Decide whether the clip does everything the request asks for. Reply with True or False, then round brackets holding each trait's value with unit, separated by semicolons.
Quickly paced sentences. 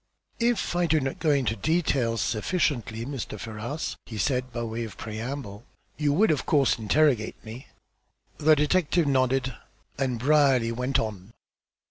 False (145 wpm)